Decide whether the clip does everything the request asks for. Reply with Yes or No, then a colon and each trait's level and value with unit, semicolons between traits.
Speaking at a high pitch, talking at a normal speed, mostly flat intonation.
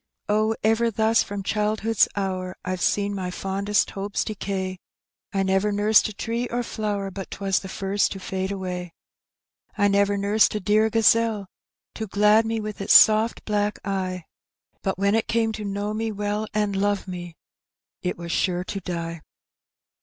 Yes: high, 205 Hz; average, 170 wpm; narrow, 2.0 semitones